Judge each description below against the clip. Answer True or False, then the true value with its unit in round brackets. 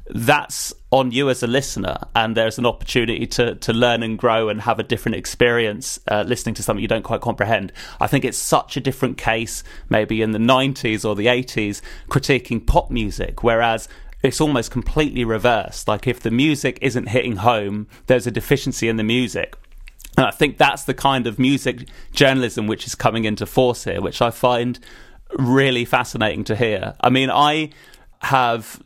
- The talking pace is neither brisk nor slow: True (190 wpm)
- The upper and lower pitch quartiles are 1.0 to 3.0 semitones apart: True (2.7 semitones)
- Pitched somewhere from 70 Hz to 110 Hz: False (120 Hz)